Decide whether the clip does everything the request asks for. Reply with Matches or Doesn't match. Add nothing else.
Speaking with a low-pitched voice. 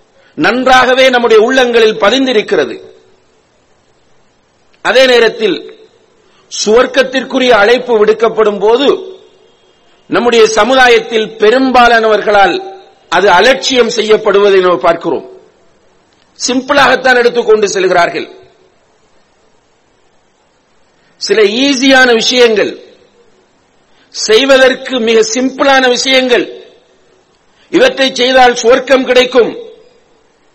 Doesn't match